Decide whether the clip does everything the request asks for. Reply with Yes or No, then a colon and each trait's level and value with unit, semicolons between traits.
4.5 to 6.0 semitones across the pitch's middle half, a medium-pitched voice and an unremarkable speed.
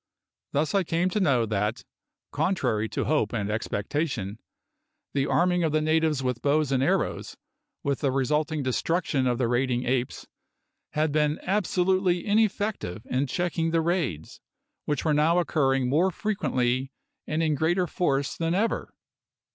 Yes: average, 5.1 semitones; medium, 150 Hz; average, 145 wpm